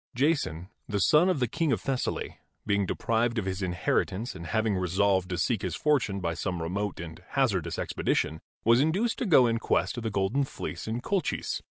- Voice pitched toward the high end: No, low, 105 Hz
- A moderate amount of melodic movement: No, wide, 6.1 semitones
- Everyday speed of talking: Yes, average, 195 wpm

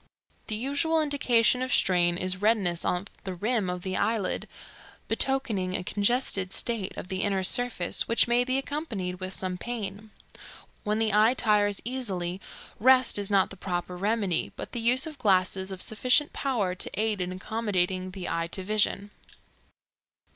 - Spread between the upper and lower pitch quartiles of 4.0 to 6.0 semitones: Yes, average, 4.4 semitones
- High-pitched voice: Yes, high, 205 Hz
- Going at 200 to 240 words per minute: No, average, 160 wpm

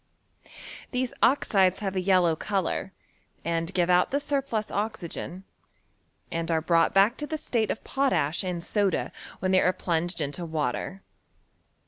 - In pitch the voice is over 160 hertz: Yes, medium, 185 Hz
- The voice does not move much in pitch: No, average, 4.3 semitones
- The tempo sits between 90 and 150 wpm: Yes, average, 145 wpm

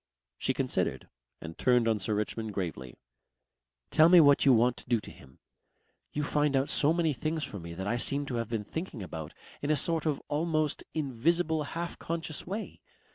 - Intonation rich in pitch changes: Yes, wide, 6.2 semitones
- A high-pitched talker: No, medium, 140 Hz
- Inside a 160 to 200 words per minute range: Yes, average, 190 wpm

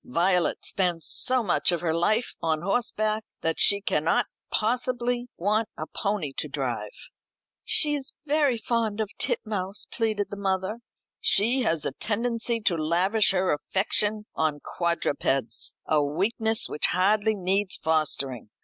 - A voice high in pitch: Yes, high, 200 Hz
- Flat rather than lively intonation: No, average, 4.9 semitones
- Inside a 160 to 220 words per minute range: No, average, 140 wpm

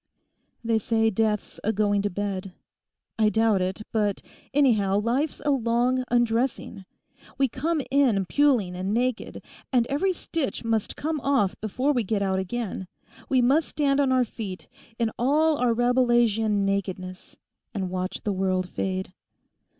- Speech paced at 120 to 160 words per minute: Yes, average, 150 wpm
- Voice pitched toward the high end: Yes, high, 225 Hz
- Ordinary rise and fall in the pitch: Yes, average, 4.5 semitones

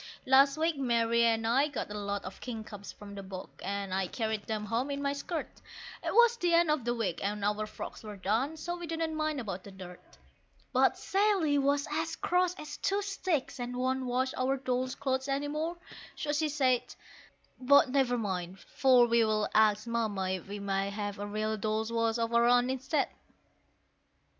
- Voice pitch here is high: Yes, high, 245 Hz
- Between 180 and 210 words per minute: Yes, average, 190 wpm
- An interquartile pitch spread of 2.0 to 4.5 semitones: No, wide, 5.4 semitones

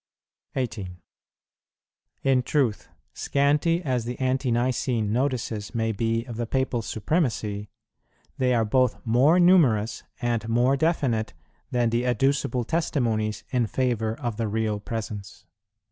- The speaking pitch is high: No, low, 120 Hz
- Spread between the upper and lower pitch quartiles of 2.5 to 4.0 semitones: Yes, average, 3.0 semitones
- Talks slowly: Yes, slow, 125 wpm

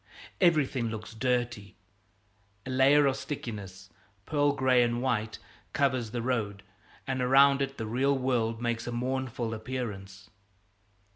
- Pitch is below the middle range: Yes, low, 125 Hz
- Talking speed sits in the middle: No, slow, 130 wpm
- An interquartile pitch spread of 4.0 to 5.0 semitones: No, average, 2.9 semitones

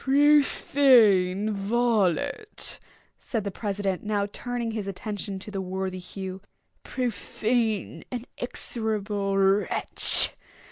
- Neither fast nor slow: No, slow, 95 wpm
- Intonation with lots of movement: No, average, 3.5 semitones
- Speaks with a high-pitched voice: Yes, high, 210 Hz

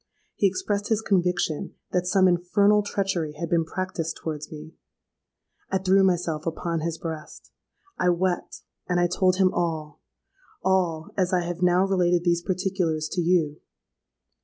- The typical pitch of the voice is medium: Yes, medium, 175 Hz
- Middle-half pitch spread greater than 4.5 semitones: No, narrow, 2.4 semitones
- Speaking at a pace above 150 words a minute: No, average, 140 wpm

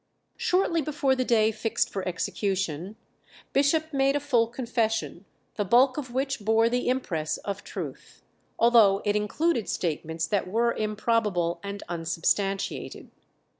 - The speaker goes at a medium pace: No, slow, 130 wpm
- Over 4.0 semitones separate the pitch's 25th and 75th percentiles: Yes, average, 4.7 semitones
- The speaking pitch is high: Yes, high, 220 Hz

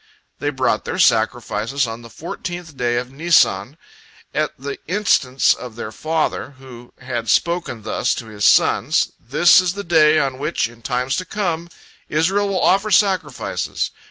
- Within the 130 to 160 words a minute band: Yes, average, 155 wpm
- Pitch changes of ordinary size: No, wide, 6.3 semitones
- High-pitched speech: No, medium, 140 Hz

